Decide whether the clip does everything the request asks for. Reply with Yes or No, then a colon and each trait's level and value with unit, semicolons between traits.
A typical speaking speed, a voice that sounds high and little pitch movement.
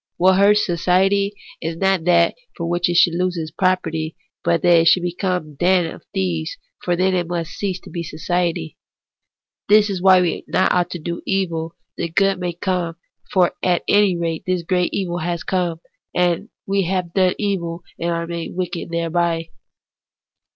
No: average, 175 wpm; medium, 175 Hz; narrow, 1.7 semitones